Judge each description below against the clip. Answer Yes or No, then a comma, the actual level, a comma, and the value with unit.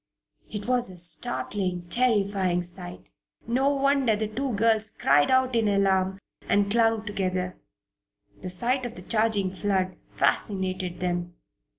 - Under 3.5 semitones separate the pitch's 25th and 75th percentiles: No, average, 3.9 semitones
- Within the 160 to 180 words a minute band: No, slow, 135 wpm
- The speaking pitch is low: No, high, 200 Hz